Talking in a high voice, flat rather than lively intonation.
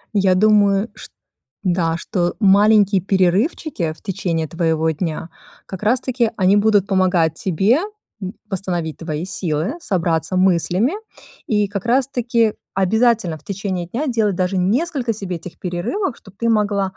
No: high, 195 Hz; average, 3.7 semitones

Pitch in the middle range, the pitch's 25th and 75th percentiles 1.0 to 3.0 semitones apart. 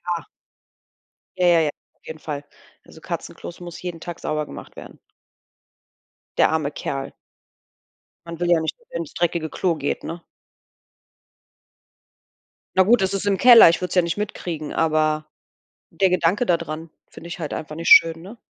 Yes: medium, 170 Hz; average, 2.7 semitones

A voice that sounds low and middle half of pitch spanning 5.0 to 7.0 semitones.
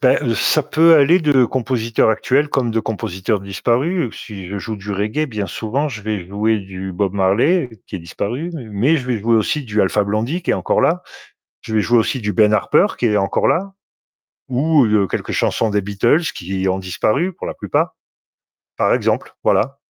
Yes: low, 110 Hz; wide, 5.6 semitones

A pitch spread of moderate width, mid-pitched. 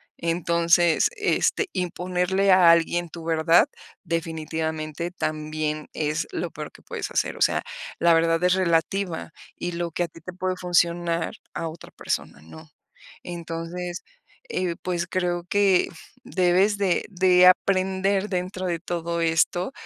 No: narrow, 1.8 semitones; medium, 175 Hz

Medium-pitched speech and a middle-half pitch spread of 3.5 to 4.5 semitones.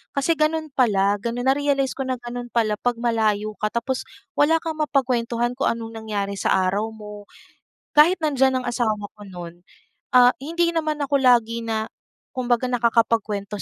No: high, 240 Hz; average, 4.1 semitones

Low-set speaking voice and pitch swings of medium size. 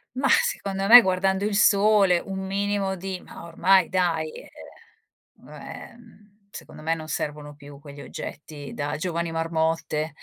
No: medium, 180 Hz; average, 4.0 semitones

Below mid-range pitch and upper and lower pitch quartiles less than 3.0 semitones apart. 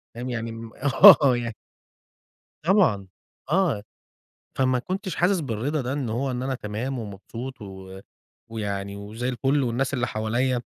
No: low, 125 Hz; average, 3.7 semitones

